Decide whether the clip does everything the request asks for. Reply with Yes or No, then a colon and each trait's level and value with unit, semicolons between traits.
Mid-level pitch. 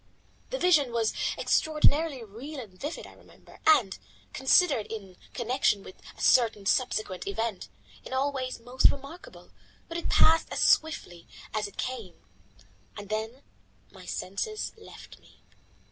No: very high, 250 Hz